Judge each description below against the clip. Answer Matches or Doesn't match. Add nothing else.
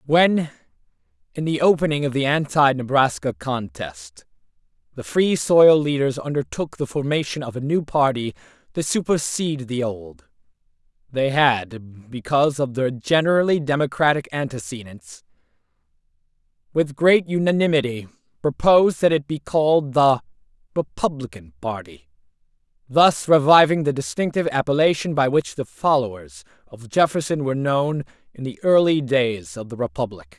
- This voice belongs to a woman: Doesn't match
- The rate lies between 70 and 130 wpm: Matches